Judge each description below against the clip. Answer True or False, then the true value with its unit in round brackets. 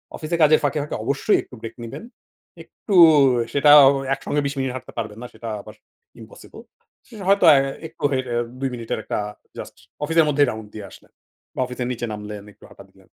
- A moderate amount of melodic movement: True (4.4 semitones)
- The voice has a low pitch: True (130 Hz)